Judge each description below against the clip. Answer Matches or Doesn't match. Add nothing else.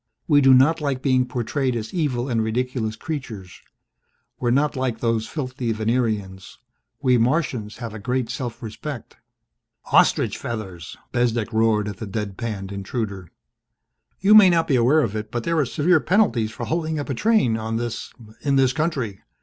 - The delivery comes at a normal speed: Matches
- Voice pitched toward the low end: Matches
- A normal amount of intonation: Matches